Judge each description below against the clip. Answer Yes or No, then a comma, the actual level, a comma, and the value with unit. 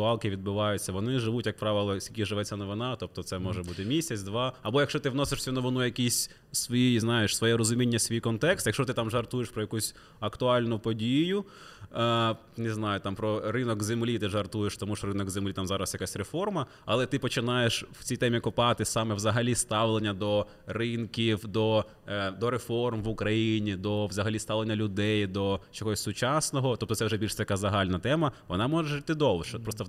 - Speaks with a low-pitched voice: Yes, low, 110 Hz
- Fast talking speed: Yes, fast, 185 wpm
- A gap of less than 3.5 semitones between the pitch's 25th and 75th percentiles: Yes, average, 2.8 semitones